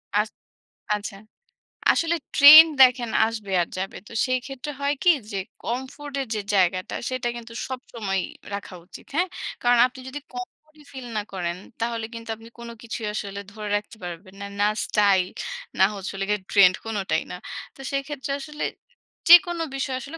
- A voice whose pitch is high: Yes, high, 230 Hz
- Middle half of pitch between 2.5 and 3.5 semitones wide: No, average, 5.2 semitones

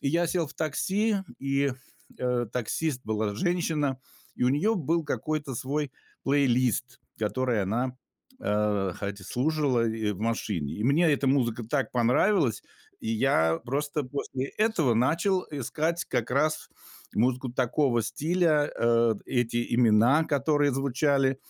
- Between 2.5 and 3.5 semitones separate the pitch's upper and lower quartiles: No, average, 4.4 semitones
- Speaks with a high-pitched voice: No, low, 130 Hz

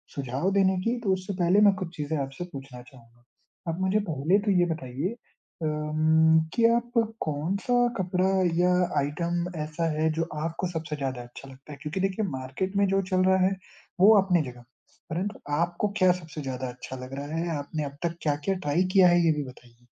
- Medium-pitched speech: Yes, medium, 160 Hz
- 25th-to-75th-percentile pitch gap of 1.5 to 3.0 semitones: No, average, 4.9 semitones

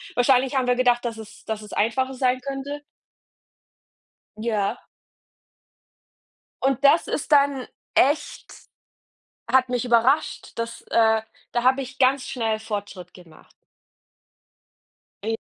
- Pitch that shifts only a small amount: No, average, 3.2 semitones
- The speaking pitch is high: Yes, high, 245 Hz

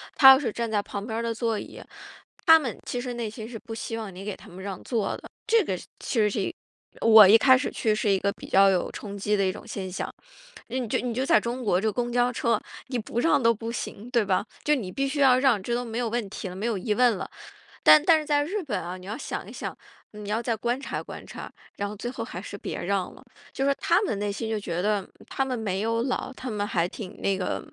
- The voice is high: Yes, high, 225 Hz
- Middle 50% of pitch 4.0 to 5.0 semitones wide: No, average, 3.6 semitones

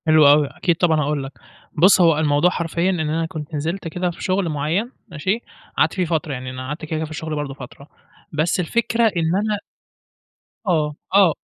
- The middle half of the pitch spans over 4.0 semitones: No, average, 3.2 semitones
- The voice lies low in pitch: No, medium, 160 Hz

